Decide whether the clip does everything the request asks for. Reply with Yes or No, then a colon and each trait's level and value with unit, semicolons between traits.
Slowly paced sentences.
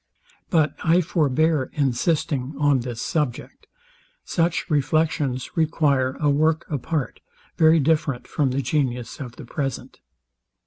Yes: slow, 120 wpm